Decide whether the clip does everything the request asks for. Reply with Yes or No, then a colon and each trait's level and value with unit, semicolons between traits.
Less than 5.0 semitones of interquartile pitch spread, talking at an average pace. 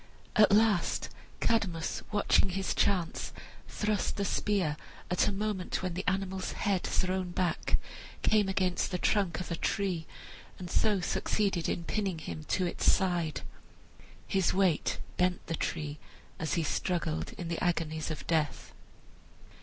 Yes: average, 2.8 semitones; average, 145 wpm